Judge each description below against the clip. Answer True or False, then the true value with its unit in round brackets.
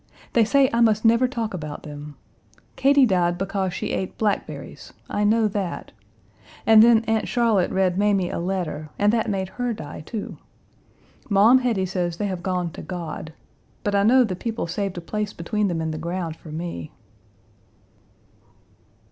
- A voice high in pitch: True (195 Hz)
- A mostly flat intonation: False (4.2 semitones)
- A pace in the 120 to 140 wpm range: False (170 wpm)